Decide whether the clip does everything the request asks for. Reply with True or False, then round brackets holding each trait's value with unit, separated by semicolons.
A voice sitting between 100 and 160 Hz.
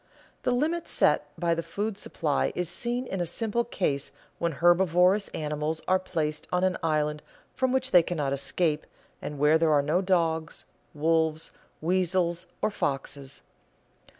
False (170 Hz)